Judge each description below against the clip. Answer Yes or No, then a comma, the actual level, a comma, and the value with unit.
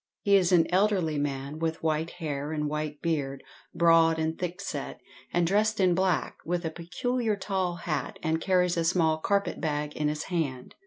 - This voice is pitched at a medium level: Yes, medium, 165 Hz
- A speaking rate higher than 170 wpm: Yes, average, 180 wpm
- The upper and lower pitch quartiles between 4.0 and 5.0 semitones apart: No, average, 3.0 semitones